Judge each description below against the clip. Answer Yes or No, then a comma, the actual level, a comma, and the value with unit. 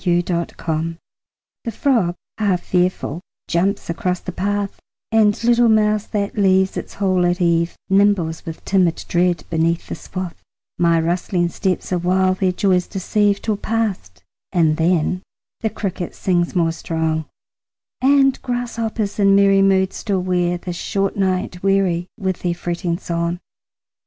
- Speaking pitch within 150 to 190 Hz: Yes, medium, 185 Hz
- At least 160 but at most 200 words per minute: No, average, 140 wpm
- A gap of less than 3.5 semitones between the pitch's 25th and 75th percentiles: Yes, average, 2.7 semitones